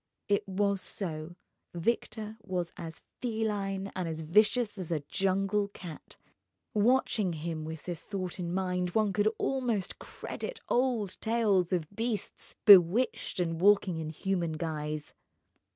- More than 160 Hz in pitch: Yes, high, 190 Hz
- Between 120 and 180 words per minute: Yes, slow, 135 wpm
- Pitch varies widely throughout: No, average, 3.8 semitones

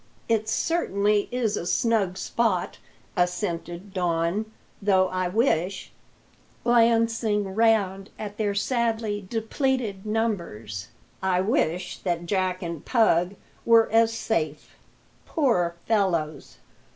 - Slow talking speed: Yes, slow, 105 wpm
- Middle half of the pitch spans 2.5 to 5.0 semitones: Yes, average, 4.0 semitones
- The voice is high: Yes, high, 200 Hz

